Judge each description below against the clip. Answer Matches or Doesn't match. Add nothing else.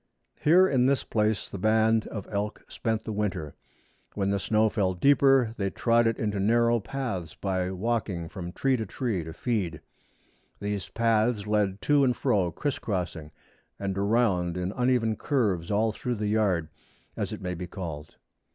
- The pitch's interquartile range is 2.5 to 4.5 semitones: Matches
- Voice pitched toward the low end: Matches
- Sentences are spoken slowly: Doesn't match